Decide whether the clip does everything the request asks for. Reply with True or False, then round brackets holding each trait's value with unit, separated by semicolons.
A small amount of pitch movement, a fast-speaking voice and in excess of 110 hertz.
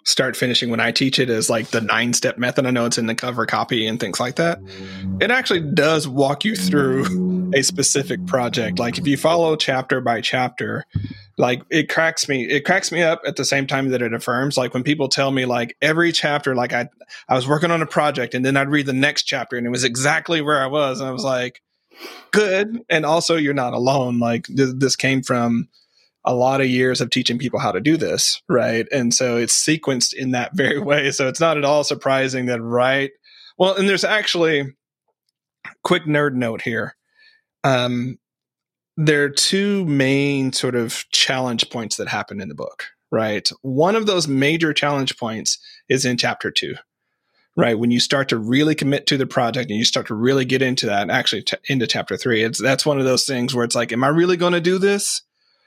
False (3.6 semitones; 215 wpm; 135 Hz)